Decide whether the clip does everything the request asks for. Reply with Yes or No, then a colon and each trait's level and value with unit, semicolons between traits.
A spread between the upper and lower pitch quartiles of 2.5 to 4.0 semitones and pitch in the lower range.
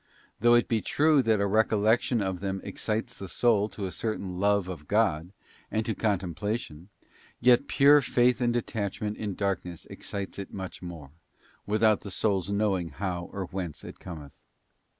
Yes: average, 3.3 semitones; low, 100 Hz